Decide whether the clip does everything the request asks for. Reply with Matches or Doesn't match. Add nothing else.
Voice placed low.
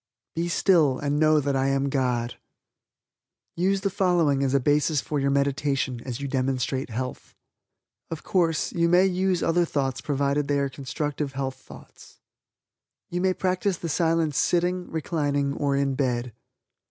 Doesn't match